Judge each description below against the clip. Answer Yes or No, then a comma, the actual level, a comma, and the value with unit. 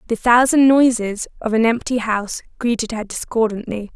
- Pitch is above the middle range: Yes, high, 230 Hz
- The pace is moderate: Yes, average, 150 wpm